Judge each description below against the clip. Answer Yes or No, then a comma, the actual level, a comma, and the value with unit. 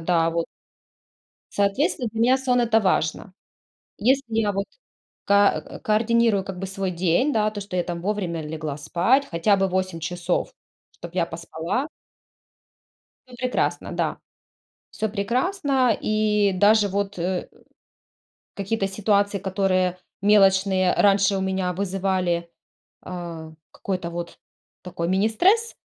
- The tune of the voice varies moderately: Yes, average, 3.2 semitones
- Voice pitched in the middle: No, high, 195 Hz